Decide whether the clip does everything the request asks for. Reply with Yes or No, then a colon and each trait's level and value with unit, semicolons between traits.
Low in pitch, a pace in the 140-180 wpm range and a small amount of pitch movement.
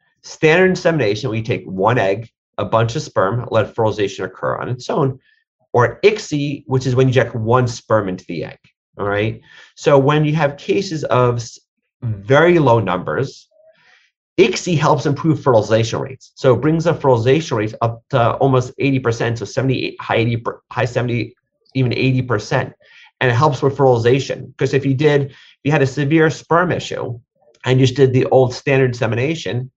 No: low, 130 Hz; average, 175 wpm; average, 3.8 semitones